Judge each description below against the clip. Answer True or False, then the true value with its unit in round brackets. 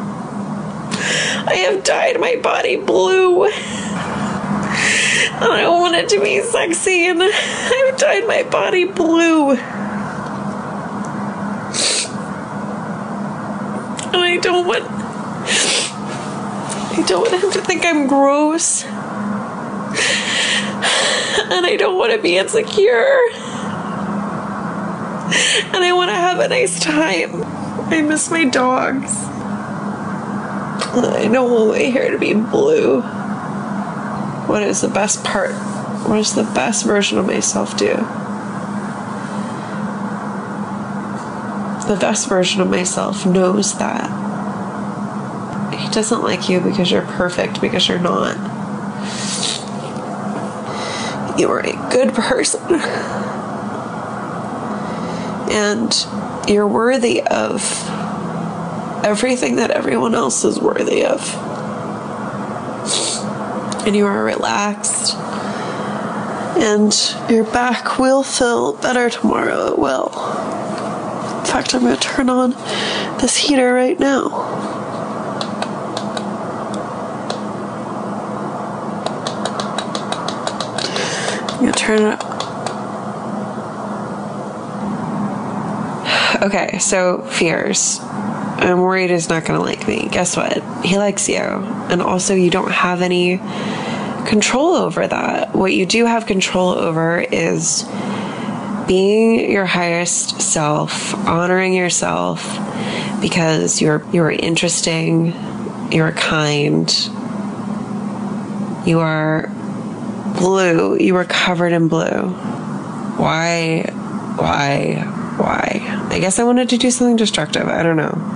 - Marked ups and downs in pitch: False (3.5 semitones)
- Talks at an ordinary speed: False (100 wpm)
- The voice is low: False (215 Hz)